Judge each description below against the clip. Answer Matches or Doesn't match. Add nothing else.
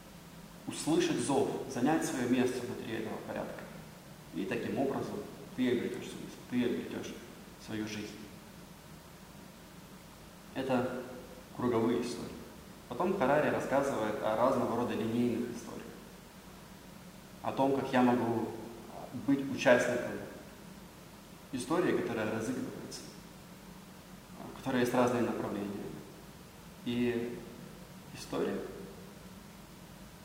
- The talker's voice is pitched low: Matches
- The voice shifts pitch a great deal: Matches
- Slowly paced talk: Matches